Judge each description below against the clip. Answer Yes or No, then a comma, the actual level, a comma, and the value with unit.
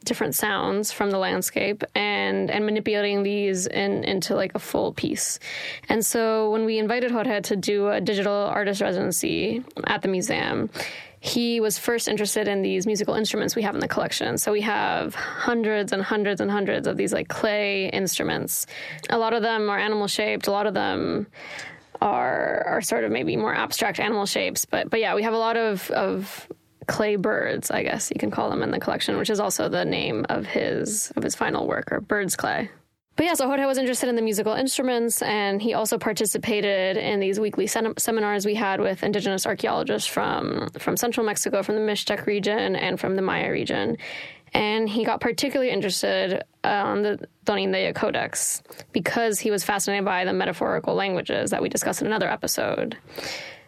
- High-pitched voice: Yes, high, 210 Hz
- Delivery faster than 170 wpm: Yes, average, 190 wpm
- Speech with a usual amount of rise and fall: No, narrow, 2.0 semitones